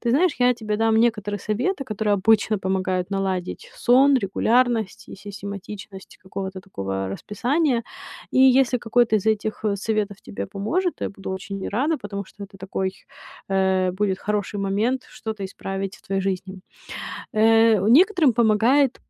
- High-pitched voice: Yes, high, 210 Hz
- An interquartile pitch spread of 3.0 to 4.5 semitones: Yes, average, 3.7 semitones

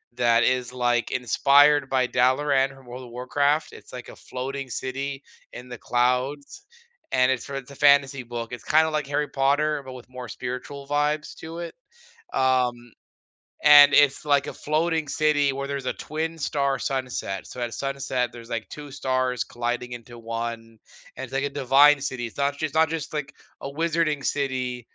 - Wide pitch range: No, average, 2.7 semitones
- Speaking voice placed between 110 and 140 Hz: Yes, low, 135 Hz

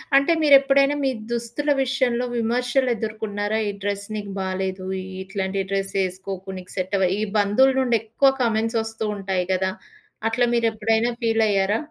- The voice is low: No, high, 220 Hz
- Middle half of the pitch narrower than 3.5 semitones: No, average, 3.8 semitones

